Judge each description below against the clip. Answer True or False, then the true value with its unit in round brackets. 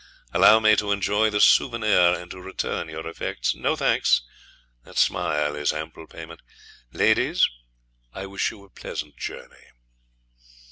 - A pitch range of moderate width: True (4.3 semitones)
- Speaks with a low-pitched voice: True (90 Hz)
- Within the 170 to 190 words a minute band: False (140 wpm)